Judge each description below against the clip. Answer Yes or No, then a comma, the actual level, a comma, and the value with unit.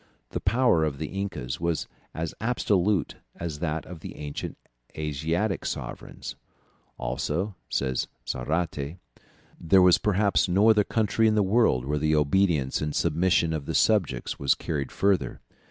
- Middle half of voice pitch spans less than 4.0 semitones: No, average, 4.9 semitones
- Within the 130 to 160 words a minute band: Yes, average, 145 wpm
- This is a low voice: Yes, very low, 85 Hz